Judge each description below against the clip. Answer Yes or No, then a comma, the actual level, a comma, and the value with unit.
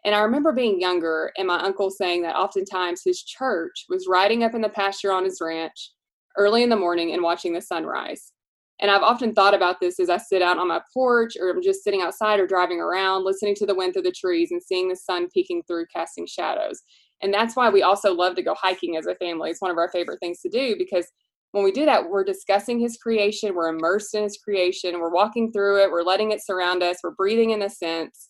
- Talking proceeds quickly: Yes, fast, 240 wpm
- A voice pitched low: No, high, 195 Hz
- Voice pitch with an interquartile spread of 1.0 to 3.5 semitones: No, average, 4.1 semitones